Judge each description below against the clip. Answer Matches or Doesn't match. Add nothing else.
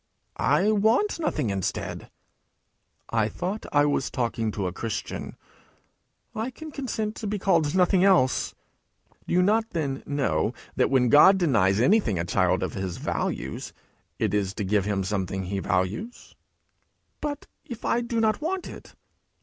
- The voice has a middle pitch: Matches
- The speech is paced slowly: Doesn't match